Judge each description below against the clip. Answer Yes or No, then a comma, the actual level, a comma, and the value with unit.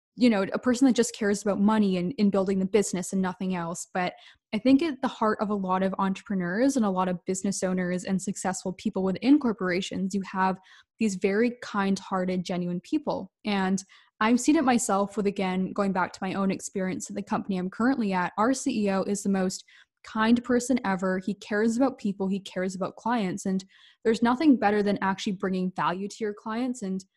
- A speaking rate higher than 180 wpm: Yes, fast, 205 wpm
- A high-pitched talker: Yes, high, 200 Hz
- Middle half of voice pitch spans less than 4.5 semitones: Yes, average, 2.9 semitones